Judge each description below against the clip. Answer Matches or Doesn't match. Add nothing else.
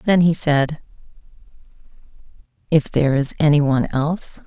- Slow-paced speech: Matches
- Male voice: Doesn't match